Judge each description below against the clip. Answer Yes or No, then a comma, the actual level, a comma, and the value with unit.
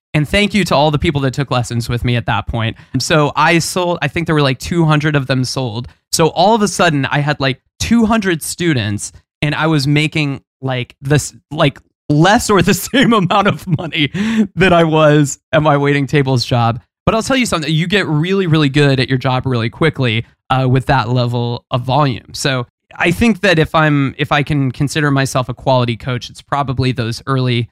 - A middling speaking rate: No, fast, 215 wpm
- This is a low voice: No, medium, 145 Hz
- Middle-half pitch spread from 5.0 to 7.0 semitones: No, average, 4.3 semitones